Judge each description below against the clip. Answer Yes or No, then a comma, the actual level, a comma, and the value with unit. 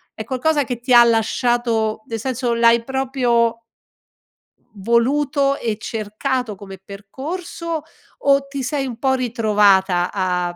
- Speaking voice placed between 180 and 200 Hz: No, high, 235 Hz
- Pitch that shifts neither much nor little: Yes, average, 3.7 semitones